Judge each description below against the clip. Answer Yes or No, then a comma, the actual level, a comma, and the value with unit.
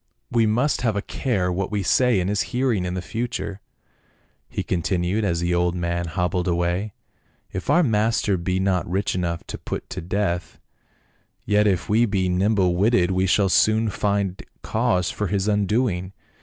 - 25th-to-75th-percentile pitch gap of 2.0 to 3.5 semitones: Yes, average, 3.2 semitones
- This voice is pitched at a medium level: No, very low, 95 Hz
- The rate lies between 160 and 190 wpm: Yes, average, 180 wpm